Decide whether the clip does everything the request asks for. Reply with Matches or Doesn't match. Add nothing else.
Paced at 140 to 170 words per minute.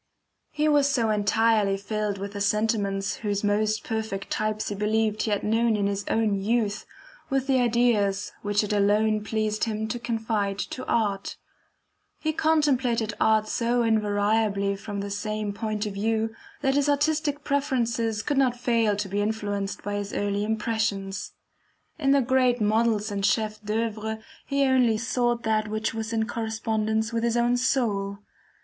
Matches